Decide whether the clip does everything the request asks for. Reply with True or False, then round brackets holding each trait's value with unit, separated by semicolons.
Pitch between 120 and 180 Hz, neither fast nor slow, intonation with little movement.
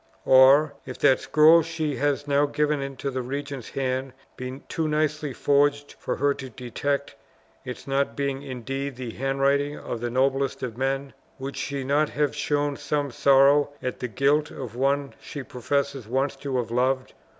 True (140 Hz; 170 wpm; 1.7 semitones)